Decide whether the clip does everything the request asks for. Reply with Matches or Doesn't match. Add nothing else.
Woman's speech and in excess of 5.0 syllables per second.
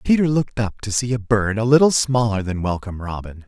Doesn't match